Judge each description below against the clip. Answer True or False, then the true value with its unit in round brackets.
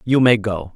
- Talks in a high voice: False (110 Hz)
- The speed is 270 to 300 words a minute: False (240 wpm)